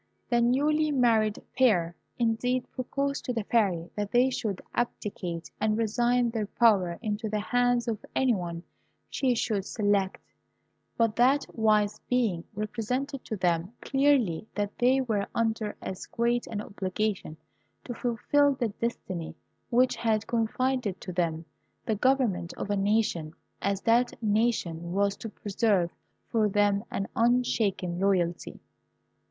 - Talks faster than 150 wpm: No, slow, 135 wpm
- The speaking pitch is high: Yes, high, 220 Hz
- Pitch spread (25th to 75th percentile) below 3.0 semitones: No, average, 3.6 semitones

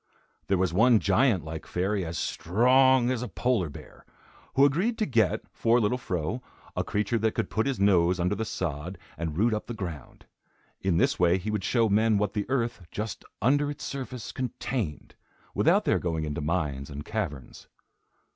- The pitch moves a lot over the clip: Yes, wide, 5.8 semitones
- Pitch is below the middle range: Yes, low, 105 Hz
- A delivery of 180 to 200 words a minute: Yes, average, 185 wpm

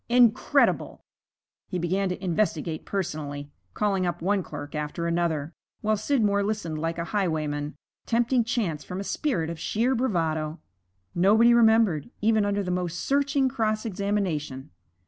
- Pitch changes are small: No, average, 5.2 semitones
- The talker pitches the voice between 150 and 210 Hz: Yes, high, 190 Hz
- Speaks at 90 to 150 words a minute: Yes, average, 140 wpm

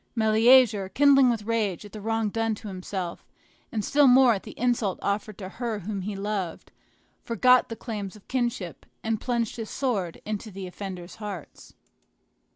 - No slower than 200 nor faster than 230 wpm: No, average, 165 wpm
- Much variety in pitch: No, average, 3.1 semitones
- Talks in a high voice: Yes, high, 215 Hz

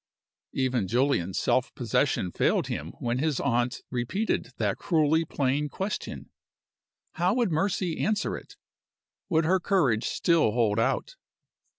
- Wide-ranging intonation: Yes, wide, 6.8 semitones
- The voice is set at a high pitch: No, medium, 150 Hz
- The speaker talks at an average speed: No, slow, 125 wpm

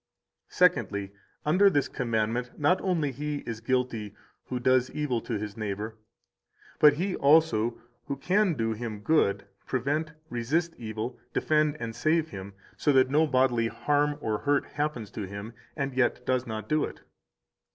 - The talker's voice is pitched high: No, low, 130 Hz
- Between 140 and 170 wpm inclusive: Yes, average, 160 wpm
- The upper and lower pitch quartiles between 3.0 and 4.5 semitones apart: No, average, 5.0 semitones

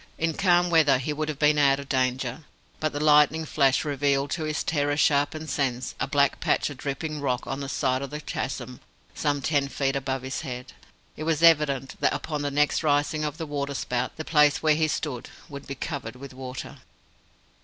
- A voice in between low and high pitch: Yes, medium, 145 Hz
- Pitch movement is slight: Yes, narrow, 2.2 semitones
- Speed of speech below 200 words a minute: No, fast, 205 wpm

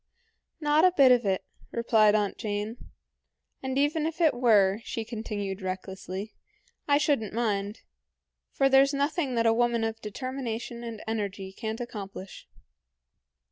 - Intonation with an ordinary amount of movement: Yes, average, 4.4 semitones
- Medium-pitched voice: No, high, 225 Hz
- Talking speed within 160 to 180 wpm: No, average, 140 wpm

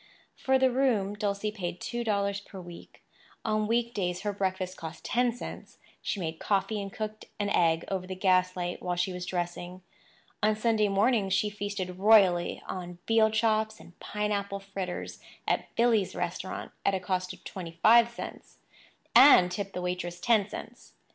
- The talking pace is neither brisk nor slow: Yes, average, 165 wpm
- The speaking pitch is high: Yes, high, 200 Hz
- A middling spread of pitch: Yes, average, 3.0 semitones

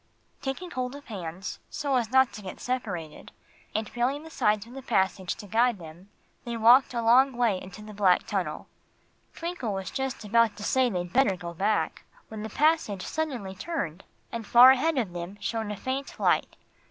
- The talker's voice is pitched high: Yes, high, 225 Hz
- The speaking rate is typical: Yes, average, 190 wpm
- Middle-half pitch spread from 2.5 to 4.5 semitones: No, average, 5.2 semitones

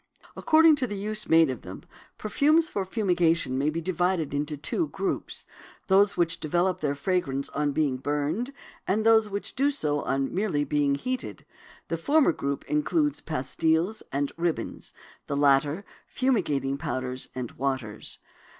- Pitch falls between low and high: Yes, medium, 165 Hz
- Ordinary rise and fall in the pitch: No, wide, 7.1 semitones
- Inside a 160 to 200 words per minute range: No, average, 150 wpm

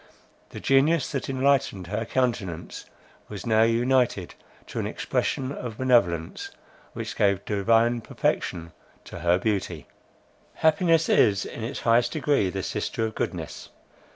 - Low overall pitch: Yes, low, 115 Hz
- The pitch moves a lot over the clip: No, average, 4.9 semitones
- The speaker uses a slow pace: Yes, slow, 130 wpm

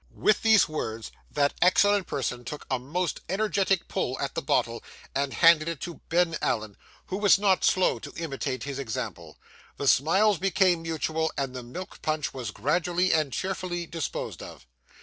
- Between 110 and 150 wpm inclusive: No, average, 170 wpm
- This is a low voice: No, medium, 160 Hz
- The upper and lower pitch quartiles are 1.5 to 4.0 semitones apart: No, wide, 5.4 semitones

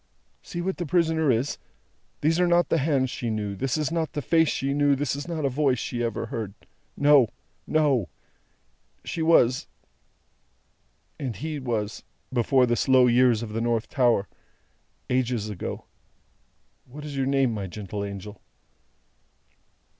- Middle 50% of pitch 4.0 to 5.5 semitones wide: Yes, average, 4.5 semitones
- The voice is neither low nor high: No, low, 130 Hz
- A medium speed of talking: Yes, average, 155 wpm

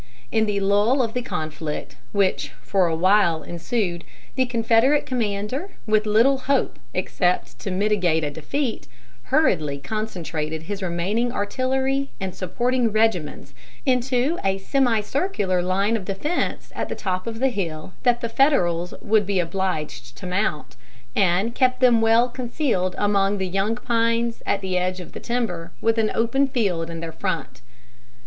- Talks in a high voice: Yes, high, 205 Hz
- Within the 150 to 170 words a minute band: Yes, average, 155 wpm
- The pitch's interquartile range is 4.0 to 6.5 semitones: Yes, average, 5.0 semitones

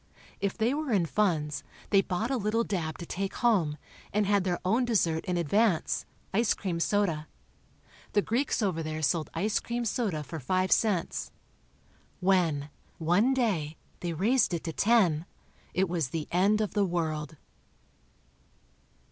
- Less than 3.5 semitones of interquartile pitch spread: No, average, 4.7 semitones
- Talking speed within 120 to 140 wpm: No, average, 150 wpm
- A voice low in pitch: No, medium, 185 Hz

